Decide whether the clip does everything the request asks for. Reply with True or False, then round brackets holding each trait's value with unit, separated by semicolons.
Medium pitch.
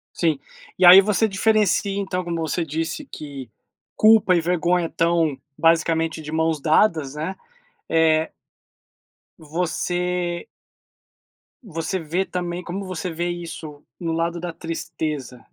True (170 Hz)